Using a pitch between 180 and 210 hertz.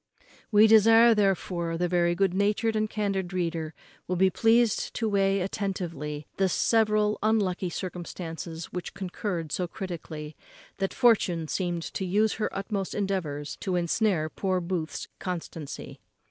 Yes: high, 190 Hz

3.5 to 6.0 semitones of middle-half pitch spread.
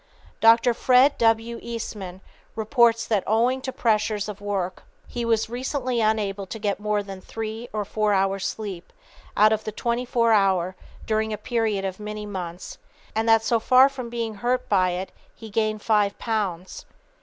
No: narrow, 2.5 semitones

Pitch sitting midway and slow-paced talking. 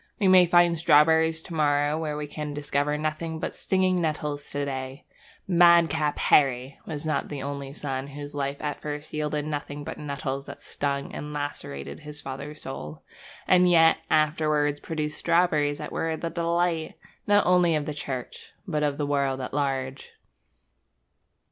No: medium, 150 Hz; average, 160 wpm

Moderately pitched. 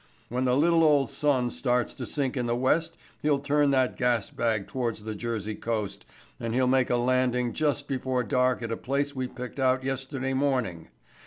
No: low, 130 Hz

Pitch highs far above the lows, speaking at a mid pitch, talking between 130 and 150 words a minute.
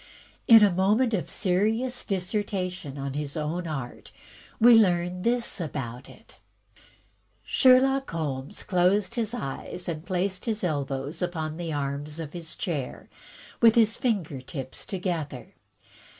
Yes: wide, 6.0 semitones; medium, 180 Hz; slow, 135 wpm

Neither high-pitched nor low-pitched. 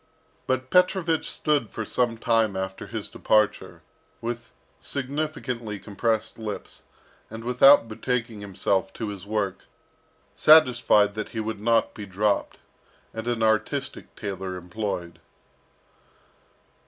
No: low, 110 Hz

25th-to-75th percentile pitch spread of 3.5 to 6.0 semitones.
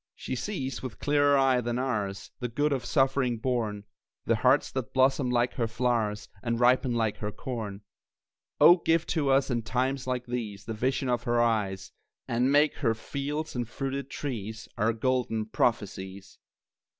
No: average, 3.1 semitones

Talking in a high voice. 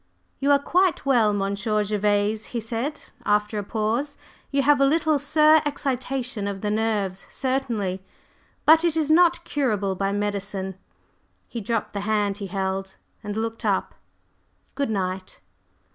Yes: high, 220 Hz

